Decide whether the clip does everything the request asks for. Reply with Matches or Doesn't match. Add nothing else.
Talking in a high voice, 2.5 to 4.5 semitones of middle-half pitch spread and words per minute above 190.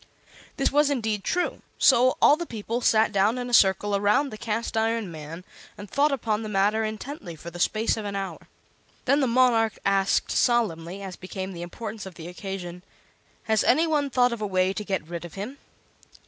Matches